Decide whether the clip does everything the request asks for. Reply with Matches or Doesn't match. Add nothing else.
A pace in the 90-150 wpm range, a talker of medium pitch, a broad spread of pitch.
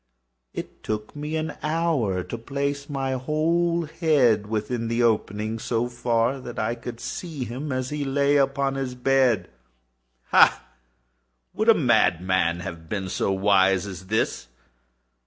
Doesn't match